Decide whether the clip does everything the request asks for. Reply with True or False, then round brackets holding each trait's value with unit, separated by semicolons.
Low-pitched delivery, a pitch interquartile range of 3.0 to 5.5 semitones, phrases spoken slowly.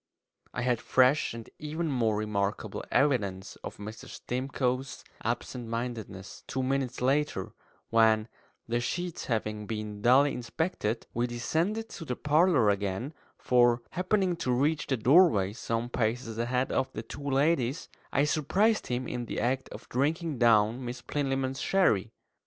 False (125 Hz; 4.1 semitones; 145 wpm)